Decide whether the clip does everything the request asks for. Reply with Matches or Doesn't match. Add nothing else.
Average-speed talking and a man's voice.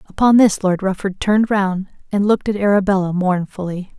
Doesn't match